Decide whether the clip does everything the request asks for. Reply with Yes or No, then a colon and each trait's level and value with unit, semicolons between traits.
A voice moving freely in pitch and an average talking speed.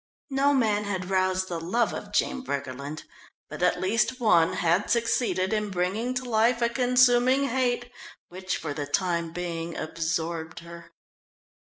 Yes: wide, 6.2 semitones; average, 150 wpm